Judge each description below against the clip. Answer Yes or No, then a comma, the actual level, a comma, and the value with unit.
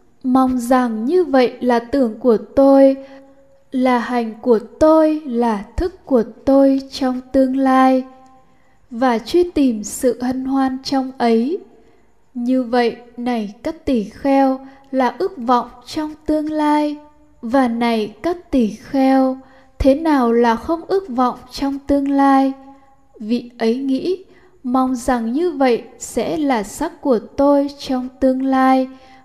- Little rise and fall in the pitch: Yes, narrow, 2.2 semitones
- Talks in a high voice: Yes, very high, 265 Hz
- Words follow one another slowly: Yes, slow, 140 wpm